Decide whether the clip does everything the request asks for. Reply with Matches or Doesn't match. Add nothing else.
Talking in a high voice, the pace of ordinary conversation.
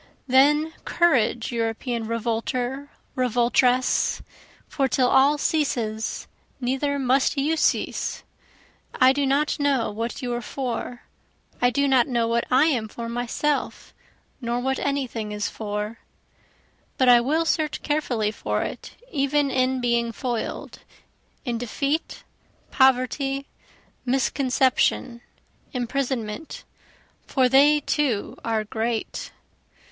Doesn't match